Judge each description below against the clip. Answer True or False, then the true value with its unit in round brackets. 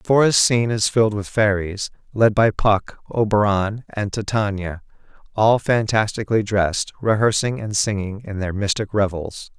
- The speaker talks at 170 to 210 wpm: False (145 wpm)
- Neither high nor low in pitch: False (105 Hz)